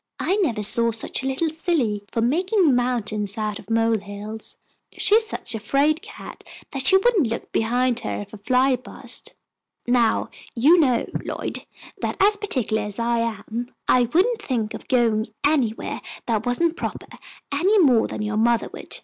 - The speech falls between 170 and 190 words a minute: Yes, average, 175 wpm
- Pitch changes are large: Yes, wide, 5.8 semitones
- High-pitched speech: Yes, high, 245 Hz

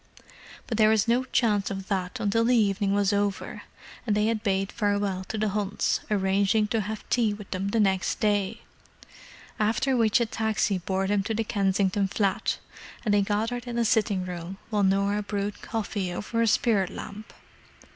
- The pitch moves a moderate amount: No, narrow, 2.0 semitones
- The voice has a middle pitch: No, high, 205 Hz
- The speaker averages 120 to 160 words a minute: No, average, 175 wpm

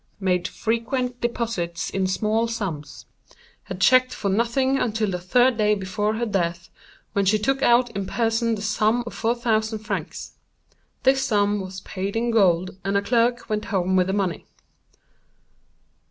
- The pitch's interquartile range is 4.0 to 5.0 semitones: No, average, 3.6 semitones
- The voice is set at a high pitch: Yes, high, 215 Hz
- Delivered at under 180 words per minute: Yes, average, 155 wpm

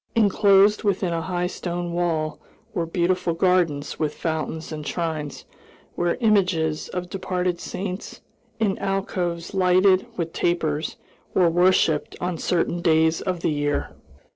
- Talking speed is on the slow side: Yes, slow, 130 wpm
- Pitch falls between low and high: Yes, medium, 175 Hz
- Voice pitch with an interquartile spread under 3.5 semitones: Yes, narrow, 2.4 semitones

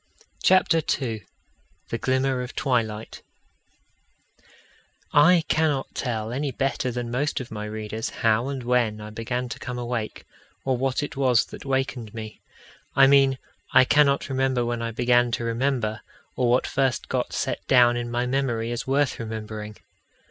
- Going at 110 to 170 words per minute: Yes, average, 155 wpm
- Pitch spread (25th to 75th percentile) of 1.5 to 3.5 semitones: Yes, average, 2.7 semitones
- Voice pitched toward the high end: No, low, 125 Hz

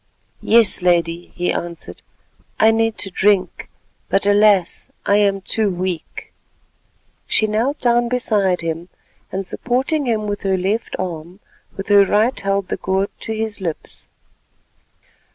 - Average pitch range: Yes, average, 3.2 semitones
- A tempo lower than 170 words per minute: Yes, slow, 135 wpm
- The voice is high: Yes, high, 200 Hz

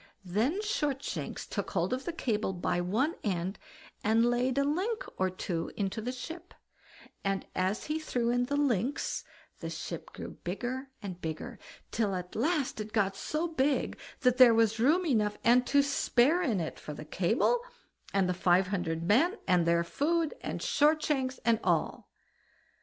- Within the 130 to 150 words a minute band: No, average, 170 wpm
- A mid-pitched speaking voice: No, high, 235 Hz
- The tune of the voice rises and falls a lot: Yes, wide, 6.9 semitones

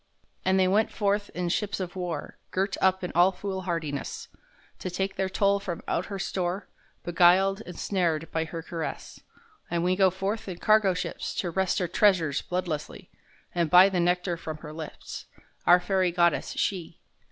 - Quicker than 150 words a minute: Yes, average, 175 wpm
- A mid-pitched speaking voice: Yes, medium, 180 Hz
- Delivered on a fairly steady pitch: Yes, narrow, 2.0 semitones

